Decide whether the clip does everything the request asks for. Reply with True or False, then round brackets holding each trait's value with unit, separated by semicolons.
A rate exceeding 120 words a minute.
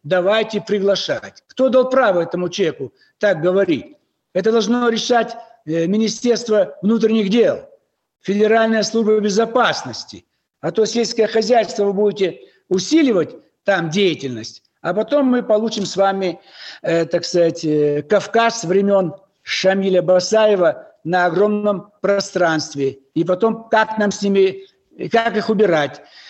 False (115 wpm)